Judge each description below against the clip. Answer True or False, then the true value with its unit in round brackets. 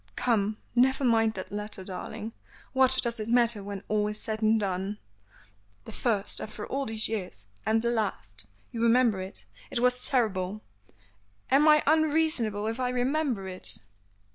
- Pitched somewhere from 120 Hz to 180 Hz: False (220 Hz)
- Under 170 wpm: True (160 wpm)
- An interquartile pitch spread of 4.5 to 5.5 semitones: False (3.4 semitones)